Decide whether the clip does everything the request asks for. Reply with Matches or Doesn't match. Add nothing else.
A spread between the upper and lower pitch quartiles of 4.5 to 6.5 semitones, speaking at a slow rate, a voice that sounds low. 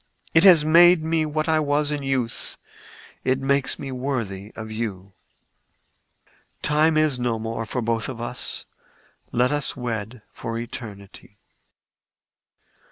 Matches